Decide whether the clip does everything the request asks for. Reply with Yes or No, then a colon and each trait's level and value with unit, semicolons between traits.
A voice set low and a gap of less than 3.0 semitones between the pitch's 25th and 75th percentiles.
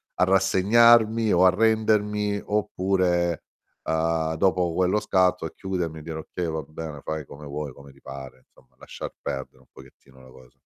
No: very low, 85 Hz; average, 4.8 semitones